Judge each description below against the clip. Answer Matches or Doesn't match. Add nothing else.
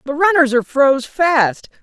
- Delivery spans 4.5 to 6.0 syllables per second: Matches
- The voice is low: Doesn't match